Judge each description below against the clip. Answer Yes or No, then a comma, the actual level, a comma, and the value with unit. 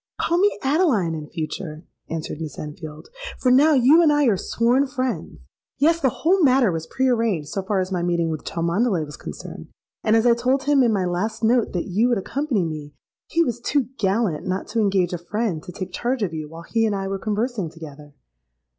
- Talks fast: Yes, fast, 215 wpm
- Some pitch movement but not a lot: No, wide, 7.0 semitones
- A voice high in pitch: Yes, high, 210 Hz